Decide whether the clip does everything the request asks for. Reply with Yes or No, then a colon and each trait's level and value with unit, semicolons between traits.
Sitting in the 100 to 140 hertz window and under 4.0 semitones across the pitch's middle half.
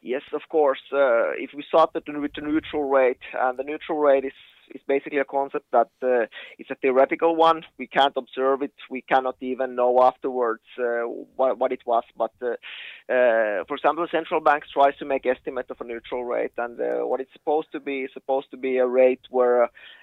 Yes: low, 135 Hz; average, 2.9 semitones